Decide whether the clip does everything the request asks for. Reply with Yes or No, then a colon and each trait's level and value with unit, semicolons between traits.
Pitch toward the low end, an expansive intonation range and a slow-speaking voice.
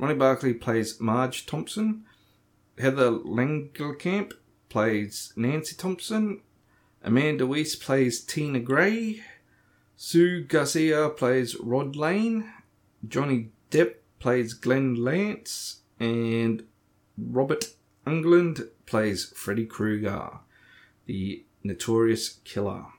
Yes: low, 125 Hz; wide, 5.8 semitones; slow, 90 wpm